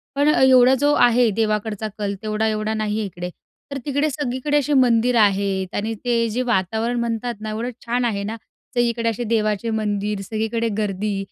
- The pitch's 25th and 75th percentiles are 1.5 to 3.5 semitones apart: Yes, narrow, 2.5 semitones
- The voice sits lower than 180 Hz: No, high, 225 Hz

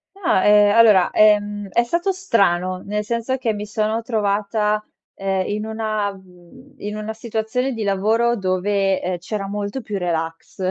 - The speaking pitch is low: No, high, 210 Hz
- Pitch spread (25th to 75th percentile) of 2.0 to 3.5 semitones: Yes, narrow, 2.5 semitones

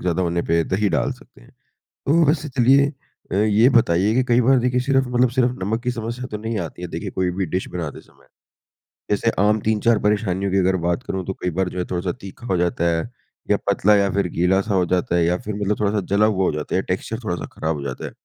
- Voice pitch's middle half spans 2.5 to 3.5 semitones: No, average, 4.4 semitones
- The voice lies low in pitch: Yes, low, 100 Hz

